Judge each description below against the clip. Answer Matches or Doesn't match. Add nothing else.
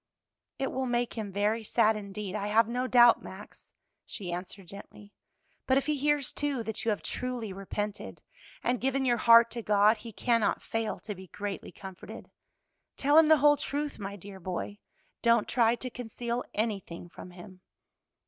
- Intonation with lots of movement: Doesn't match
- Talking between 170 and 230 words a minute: Matches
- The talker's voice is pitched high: Matches